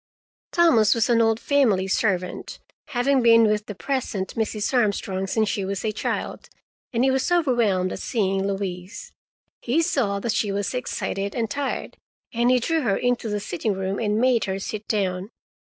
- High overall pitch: Yes, high, 215 Hz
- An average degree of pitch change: Yes, average, 3.9 semitones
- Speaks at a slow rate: No, average, 175 wpm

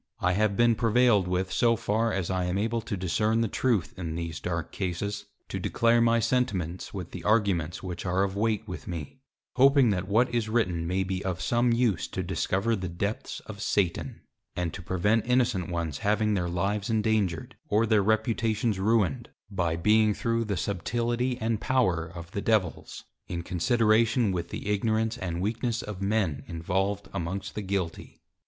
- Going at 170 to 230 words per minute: Yes, average, 175 wpm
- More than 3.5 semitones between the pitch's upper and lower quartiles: Yes, average, 3.9 semitones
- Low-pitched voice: Yes, low, 100 Hz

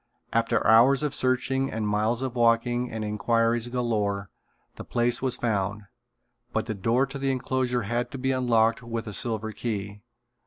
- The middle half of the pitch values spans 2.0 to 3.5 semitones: Yes, narrow, 2.5 semitones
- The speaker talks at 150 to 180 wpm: Yes, average, 165 wpm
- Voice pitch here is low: Yes, low, 115 Hz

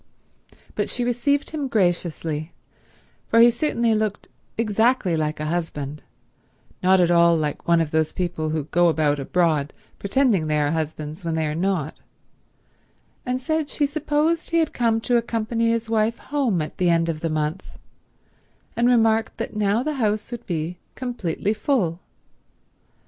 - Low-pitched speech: No, high, 195 Hz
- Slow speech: No, average, 160 wpm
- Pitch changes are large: Yes, wide, 6.7 semitones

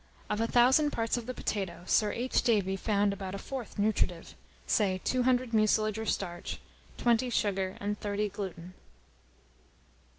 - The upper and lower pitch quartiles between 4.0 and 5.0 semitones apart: No, average, 3.2 semitones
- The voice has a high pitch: Yes, high, 210 Hz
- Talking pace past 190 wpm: No, average, 145 wpm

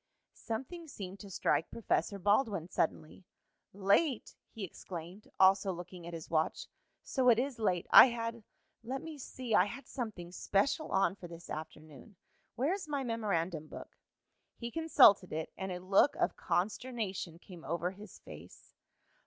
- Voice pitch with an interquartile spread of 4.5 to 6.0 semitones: Yes, average, 5.2 semitones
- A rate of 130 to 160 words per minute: Yes, average, 155 wpm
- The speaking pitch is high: Yes, high, 200 Hz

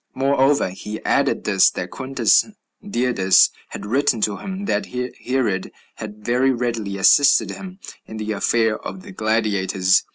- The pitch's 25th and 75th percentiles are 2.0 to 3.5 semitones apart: No, average, 4.2 semitones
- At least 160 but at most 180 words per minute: No, average, 140 wpm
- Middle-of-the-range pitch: No, low, 120 Hz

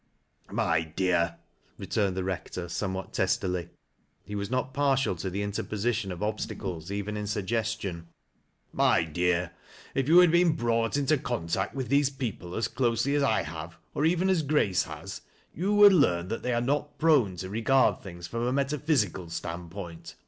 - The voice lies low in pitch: Yes, low, 105 Hz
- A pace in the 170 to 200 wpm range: Yes, average, 185 wpm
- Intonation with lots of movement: Yes, wide, 7.0 semitones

